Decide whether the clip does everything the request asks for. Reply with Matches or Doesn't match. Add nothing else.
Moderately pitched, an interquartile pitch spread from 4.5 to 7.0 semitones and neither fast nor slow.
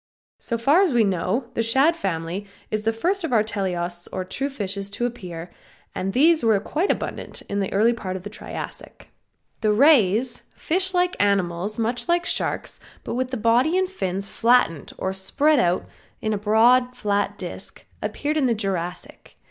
Doesn't match